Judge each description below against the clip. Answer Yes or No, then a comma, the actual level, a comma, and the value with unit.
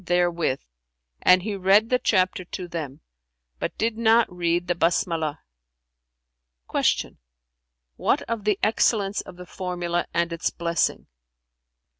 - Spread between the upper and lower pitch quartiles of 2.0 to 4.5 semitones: Yes, average, 3.8 semitones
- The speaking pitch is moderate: Yes, medium, 175 Hz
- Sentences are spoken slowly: Yes, slow, 125 wpm